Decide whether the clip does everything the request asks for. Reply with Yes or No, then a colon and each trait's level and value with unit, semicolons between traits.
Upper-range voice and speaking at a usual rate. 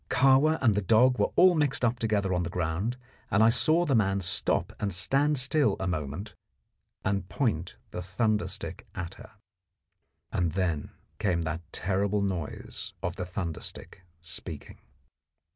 No: low, 100 Hz; average, 160 wpm